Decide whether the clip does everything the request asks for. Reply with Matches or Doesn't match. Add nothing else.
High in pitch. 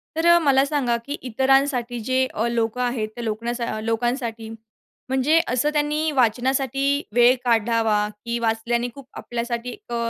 Matches